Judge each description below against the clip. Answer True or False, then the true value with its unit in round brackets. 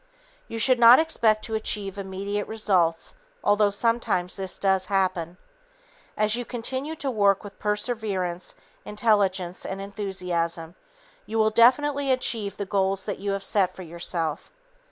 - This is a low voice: False (200 Hz)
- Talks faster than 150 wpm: False (140 wpm)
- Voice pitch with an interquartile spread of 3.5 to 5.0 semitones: False (3.0 semitones)